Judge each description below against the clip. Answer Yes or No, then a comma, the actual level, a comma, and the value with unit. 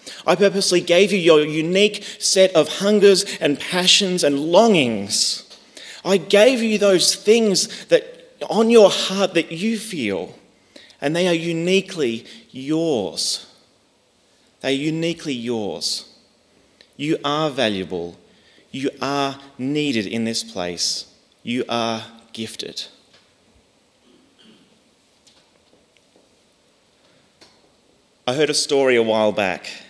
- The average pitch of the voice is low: No, medium, 155 Hz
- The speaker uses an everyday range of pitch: No, wide, 8.5 semitones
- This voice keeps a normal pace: No, slow, 105 wpm